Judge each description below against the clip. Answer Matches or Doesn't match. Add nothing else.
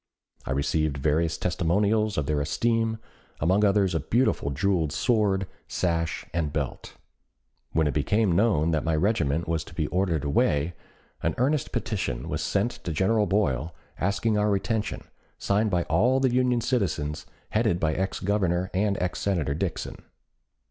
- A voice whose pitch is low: Matches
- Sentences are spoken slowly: Doesn't match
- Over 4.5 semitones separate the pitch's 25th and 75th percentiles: Matches